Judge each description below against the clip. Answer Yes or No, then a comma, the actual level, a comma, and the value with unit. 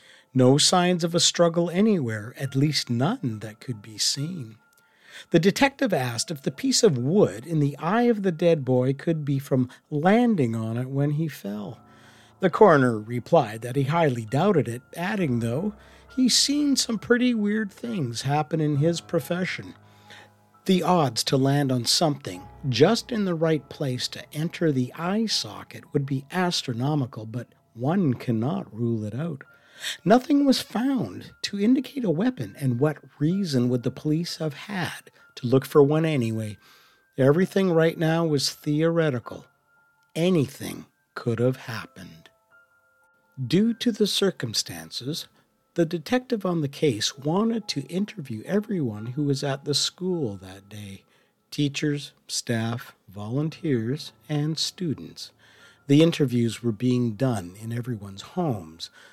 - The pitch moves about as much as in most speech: No, wide, 6.9 semitones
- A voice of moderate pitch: Yes, medium, 145 Hz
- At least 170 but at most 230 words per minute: No, average, 145 wpm